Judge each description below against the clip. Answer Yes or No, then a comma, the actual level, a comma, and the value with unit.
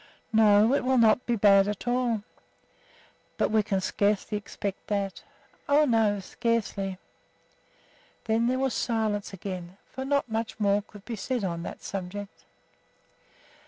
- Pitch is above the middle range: Yes, high, 210 Hz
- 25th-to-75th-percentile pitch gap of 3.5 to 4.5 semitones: No, average, 2.9 semitones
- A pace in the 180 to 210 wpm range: No, average, 140 wpm